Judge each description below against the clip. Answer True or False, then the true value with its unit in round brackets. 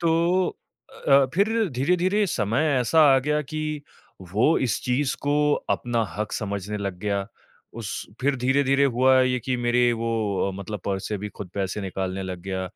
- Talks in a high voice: False (125 Hz)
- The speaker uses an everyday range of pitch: False (6.1 semitones)